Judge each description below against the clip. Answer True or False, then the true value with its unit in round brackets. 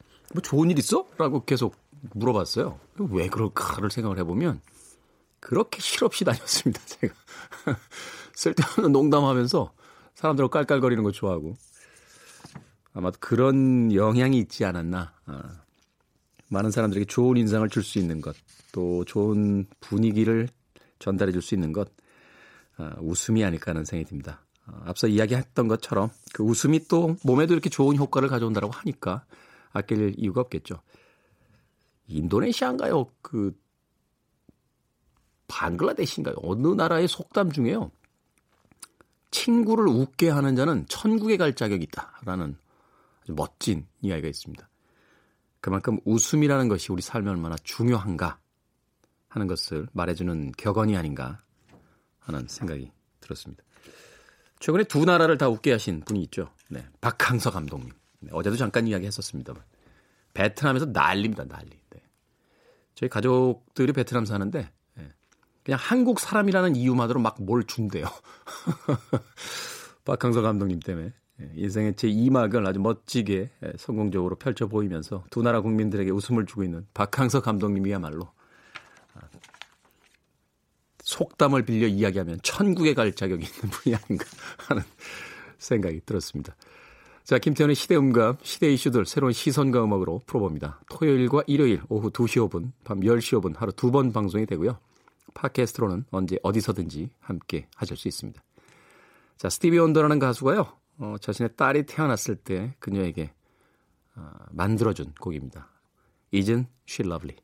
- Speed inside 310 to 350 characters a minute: True (315 characters per minute)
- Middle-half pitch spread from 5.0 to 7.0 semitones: True (5.4 semitones)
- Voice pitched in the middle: False (110 Hz)